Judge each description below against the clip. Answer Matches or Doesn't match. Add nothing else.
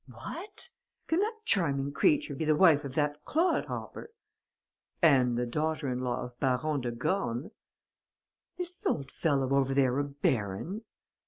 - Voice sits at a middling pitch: Matches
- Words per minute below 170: Matches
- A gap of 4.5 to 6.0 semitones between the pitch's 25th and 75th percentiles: Matches